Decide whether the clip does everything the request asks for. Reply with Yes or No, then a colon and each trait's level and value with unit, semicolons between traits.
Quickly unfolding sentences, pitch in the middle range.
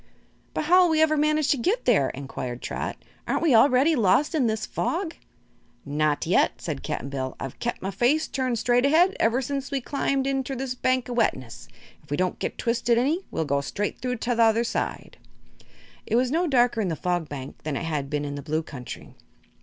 No: fast, 210 wpm; high, 240 Hz